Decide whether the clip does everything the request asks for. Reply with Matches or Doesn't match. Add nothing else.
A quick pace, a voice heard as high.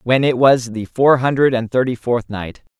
Doesn't match